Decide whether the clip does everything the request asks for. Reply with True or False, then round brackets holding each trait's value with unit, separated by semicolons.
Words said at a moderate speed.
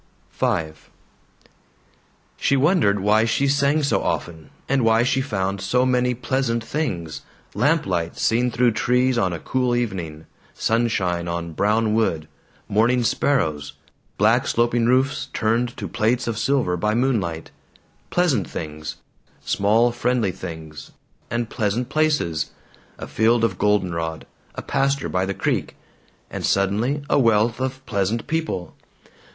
False (130 wpm)